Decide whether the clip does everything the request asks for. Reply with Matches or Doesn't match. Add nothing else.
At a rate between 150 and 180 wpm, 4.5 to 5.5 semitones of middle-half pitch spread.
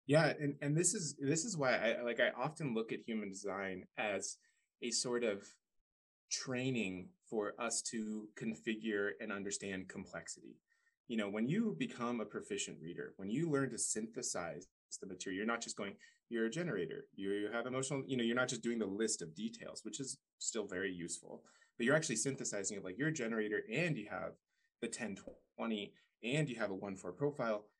Doesn't match